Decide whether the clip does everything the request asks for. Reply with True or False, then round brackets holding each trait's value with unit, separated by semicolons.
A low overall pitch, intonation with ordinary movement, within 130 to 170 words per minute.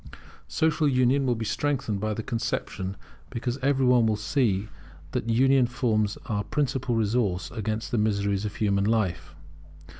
True (115 Hz; 3.6 semitones; 150 wpm)